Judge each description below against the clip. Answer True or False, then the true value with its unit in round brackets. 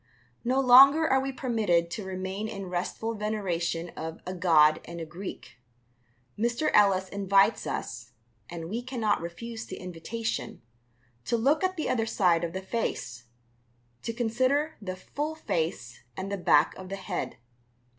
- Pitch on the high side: True (195 Hz)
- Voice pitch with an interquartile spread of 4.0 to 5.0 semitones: False (5.4 semitones)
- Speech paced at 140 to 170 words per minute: True (155 wpm)